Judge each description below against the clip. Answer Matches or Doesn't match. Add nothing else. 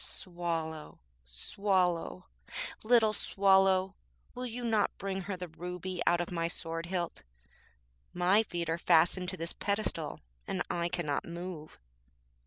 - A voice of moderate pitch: Matches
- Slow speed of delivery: Matches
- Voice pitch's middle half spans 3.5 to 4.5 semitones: Doesn't match